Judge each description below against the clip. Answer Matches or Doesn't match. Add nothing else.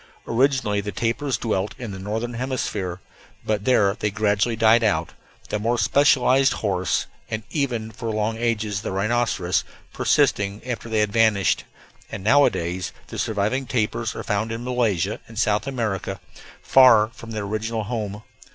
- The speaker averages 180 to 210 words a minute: Doesn't match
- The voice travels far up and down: Doesn't match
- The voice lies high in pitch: Doesn't match